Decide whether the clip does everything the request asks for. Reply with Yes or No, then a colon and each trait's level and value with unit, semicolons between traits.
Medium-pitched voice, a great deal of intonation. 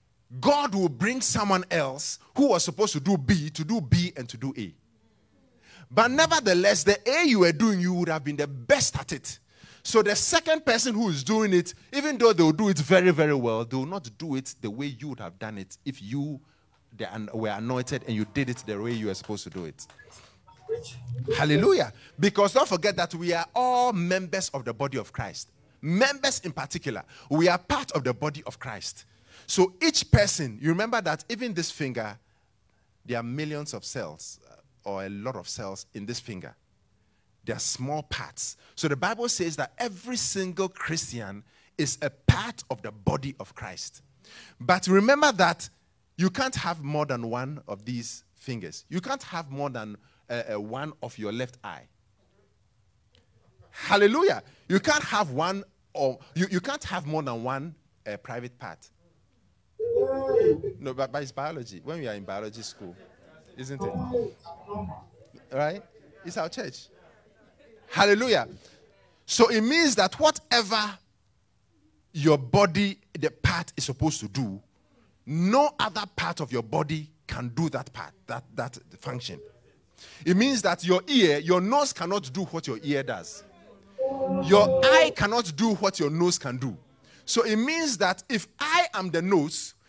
Yes: medium, 150 Hz; wide, 8.9 semitones